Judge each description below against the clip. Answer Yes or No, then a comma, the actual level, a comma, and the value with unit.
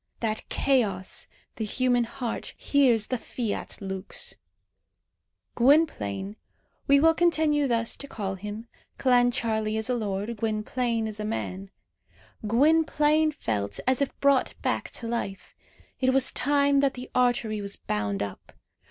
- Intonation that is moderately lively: Yes, average, 4.6 semitones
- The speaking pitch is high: Yes, high, 235 Hz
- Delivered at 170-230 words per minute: No, slow, 135 wpm